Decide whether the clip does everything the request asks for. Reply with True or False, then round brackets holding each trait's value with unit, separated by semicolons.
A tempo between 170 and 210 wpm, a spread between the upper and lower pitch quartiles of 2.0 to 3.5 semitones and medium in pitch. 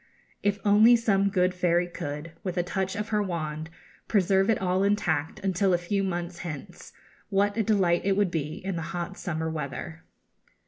True (180 wpm; 2.8 semitones; 180 Hz)